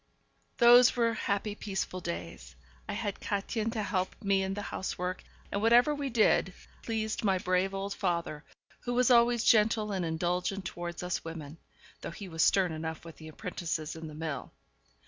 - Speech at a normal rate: Yes, average, 170 wpm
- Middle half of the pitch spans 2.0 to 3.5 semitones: No, average, 4.2 semitones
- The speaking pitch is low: No, high, 195 Hz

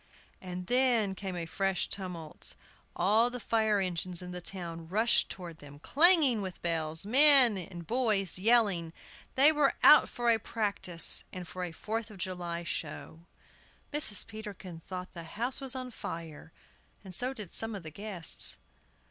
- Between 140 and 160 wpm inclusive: Yes, average, 155 wpm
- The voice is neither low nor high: No, high, 195 Hz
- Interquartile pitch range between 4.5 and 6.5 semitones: Yes, average, 5.0 semitones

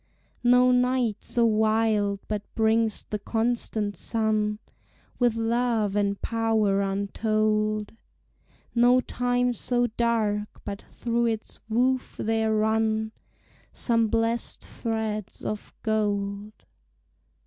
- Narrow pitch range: Yes, narrow, 1.8 semitones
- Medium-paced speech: No, slow, 100 wpm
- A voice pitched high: Yes, high, 220 Hz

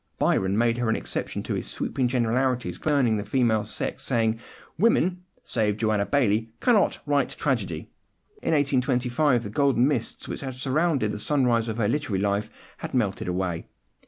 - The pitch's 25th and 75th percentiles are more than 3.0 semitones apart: Yes, average, 4.3 semitones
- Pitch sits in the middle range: No, low, 120 Hz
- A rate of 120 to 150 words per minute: No, average, 160 wpm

